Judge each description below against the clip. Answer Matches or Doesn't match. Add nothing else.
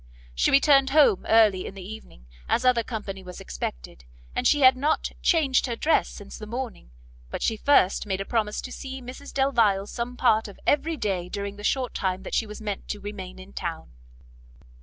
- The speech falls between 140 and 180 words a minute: Doesn't match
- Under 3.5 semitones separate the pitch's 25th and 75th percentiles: Doesn't match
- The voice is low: Doesn't match